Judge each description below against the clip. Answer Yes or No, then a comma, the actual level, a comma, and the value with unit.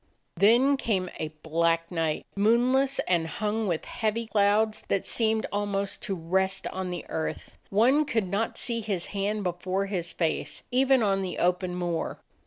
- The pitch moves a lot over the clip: No, average, 3.8 semitones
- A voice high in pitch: Yes, high, 200 Hz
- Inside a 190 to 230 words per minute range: No, average, 160 wpm